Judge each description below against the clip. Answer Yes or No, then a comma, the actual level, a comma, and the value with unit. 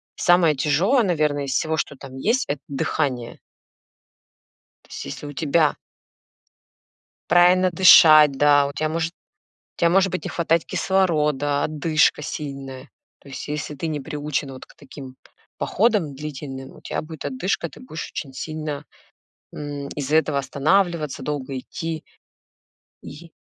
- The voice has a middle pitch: Yes, medium, 150 Hz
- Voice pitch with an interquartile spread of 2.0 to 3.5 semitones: Yes, average, 3.0 semitones